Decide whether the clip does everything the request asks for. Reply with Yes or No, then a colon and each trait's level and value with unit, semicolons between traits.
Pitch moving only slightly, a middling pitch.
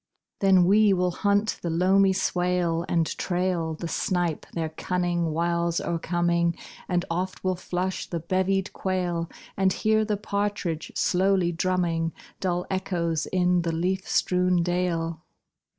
Yes: narrow, 1.8 semitones; medium, 180 Hz